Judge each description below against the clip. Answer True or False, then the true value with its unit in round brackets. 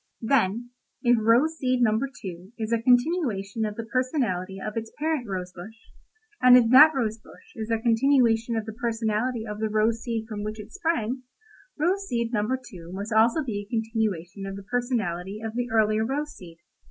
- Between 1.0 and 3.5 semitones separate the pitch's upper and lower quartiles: True (2.9 semitones)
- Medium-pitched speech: False (225 Hz)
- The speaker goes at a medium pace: True (190 wpm)